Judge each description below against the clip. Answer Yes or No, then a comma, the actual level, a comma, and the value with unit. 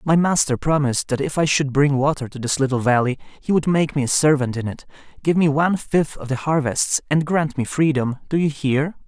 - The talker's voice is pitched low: No, medium, 145 Hz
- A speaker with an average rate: No, fast, 225 wpm